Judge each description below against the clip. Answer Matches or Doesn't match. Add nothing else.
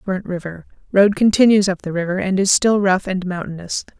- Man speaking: Doesn't match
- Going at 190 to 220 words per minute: Doesn't match